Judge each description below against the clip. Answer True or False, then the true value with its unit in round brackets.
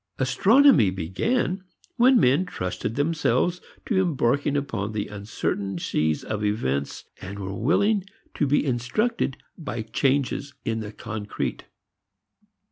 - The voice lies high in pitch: False (125 Hz)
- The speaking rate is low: True (120 wpm)